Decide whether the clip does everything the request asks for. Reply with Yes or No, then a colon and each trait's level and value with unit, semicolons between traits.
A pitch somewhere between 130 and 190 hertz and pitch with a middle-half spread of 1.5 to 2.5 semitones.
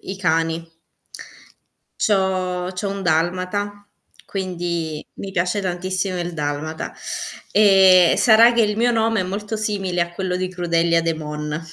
No: medium, 185 Hz; average, 2.9 semitones